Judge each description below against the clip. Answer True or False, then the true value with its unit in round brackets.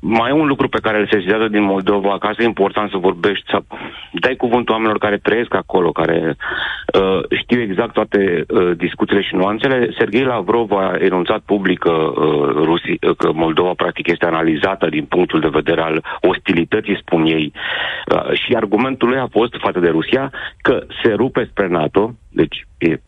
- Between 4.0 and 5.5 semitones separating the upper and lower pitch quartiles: False (3.5 semitones)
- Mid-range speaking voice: False (100 Hz)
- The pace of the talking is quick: True (175 wpm)